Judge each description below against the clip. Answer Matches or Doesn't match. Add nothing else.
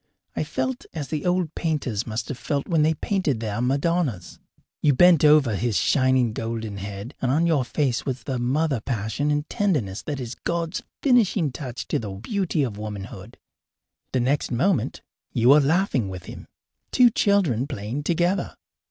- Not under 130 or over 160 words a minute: Doesn't match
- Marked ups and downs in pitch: Matches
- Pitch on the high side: Doesn't match